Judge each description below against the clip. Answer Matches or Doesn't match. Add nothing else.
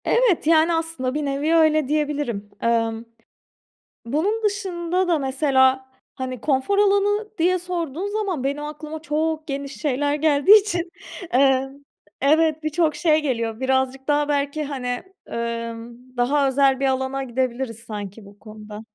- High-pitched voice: Matches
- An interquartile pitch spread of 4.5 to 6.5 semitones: Doesn't match